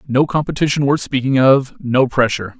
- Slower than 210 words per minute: Yes, average, 140 wpm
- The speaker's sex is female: No, male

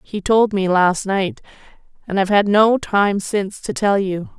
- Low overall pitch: No, high, 200 Hz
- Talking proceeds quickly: No, average, 190 wpm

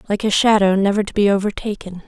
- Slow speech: No, fast, 205 wpm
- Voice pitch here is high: Yes, high, 200 Hz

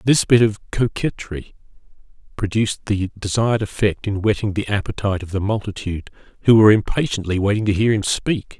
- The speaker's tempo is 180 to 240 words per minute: No, average, 160 wpm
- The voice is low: Yes, low, 105 Hz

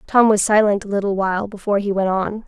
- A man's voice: No, female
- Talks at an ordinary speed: No, fast, 245 wpm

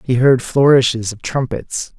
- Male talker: Yes, male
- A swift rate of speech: No, average, 150 wpm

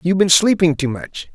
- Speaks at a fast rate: Yes, fast, 225 wpm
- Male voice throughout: Yes, male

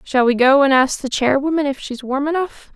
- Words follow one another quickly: Yes, fast, 260 wpm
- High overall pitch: Yes, very high, 275 Hz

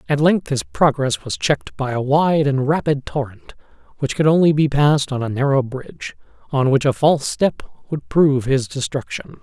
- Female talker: No, male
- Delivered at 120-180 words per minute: No, average, 190 wpm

